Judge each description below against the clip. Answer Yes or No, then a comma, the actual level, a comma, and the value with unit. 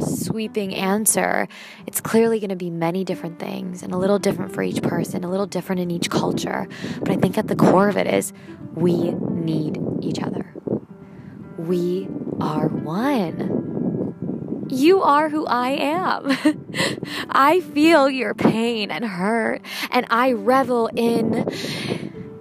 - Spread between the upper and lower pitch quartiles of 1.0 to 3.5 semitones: No, average, 4.7 semitones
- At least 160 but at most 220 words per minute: No, average, 145 wpm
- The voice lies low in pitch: No, high, 205 Hz